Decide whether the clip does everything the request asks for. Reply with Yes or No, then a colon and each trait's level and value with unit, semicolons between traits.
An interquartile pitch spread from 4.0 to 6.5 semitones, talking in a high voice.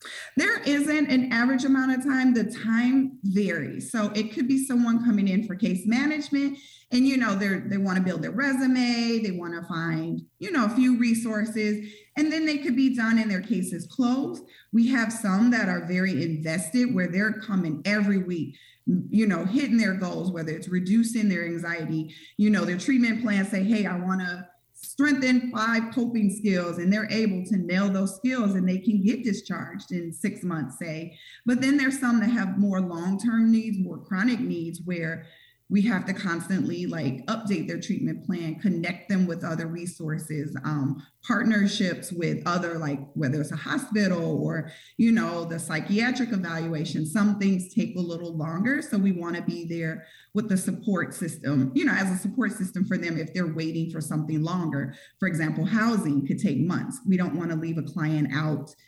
Yes: average, 5.2 semitones; high, 195 Hz